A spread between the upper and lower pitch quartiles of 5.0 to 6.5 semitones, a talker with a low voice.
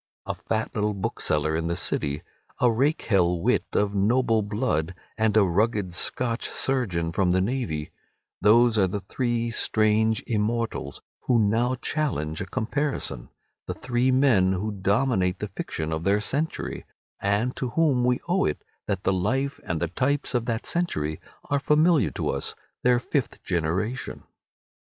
Yes: average, 5.3 semitones; low, 110 Hz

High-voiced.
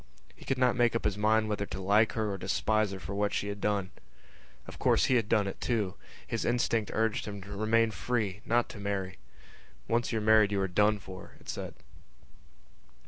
No: low, 105 Hz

